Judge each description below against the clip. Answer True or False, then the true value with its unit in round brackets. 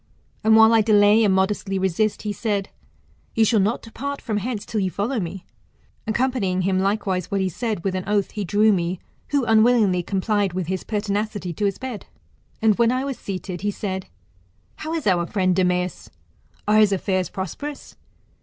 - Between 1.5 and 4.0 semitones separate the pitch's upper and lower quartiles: True (2.8 semitones)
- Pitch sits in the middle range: False (205 Hz)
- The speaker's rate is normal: True (180 wpm)